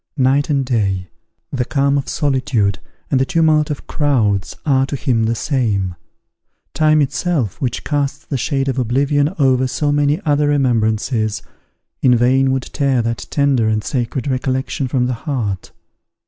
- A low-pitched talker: Yes, low, 130 Hz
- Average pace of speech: Yes, average, 155 wpm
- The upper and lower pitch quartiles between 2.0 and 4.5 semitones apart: Yes, average, 3.5 semitones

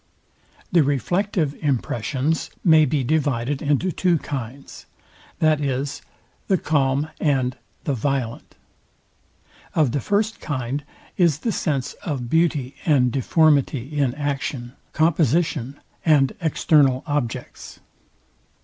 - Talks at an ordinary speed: No, slow, 105 wpm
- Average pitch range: Yes, average, 3.1 semitones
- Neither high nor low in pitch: Yes, medium, 145 Hz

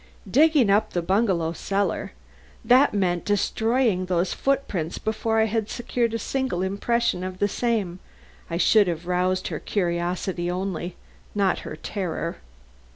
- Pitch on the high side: Yes, high, 195 Hz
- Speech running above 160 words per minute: No, average, 140 wpm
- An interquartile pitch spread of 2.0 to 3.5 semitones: No, average, 3.9 semitones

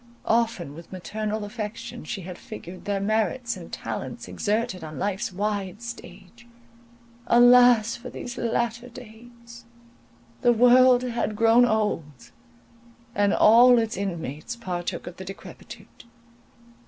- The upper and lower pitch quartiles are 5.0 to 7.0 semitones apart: No, average, 3.5 semitones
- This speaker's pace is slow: Yes, slow, 120 wpm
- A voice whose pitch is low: No, high, 220 Hz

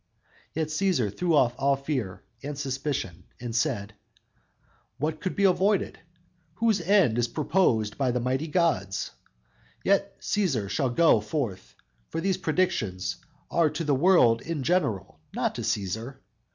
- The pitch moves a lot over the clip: Yes, wide, 7.0 semitones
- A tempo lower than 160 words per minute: Yes, average, 140 wpm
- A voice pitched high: No, medium, 140 Hz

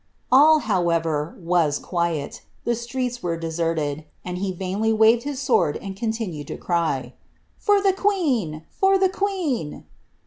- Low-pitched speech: No, high, 195 Hz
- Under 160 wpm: Yes, average, 150 wpm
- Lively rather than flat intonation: Yes, wide, 8.0 semitones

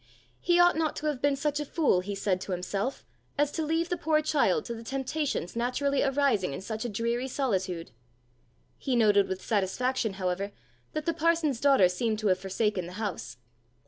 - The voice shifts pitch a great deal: Yes, wide, 6.9 semitones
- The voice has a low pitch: No, high, 235 Hz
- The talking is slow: No, average, 190 wpm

